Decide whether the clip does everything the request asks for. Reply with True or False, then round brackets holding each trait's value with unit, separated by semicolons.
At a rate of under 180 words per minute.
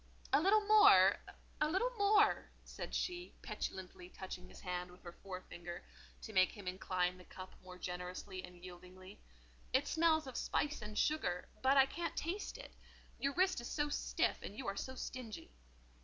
True (170 wpm)